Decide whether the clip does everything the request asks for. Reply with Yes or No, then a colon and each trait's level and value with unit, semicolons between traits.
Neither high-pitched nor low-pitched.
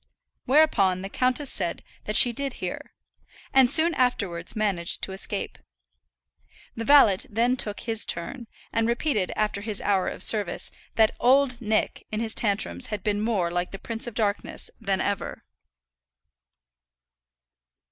No: high, 215 Hz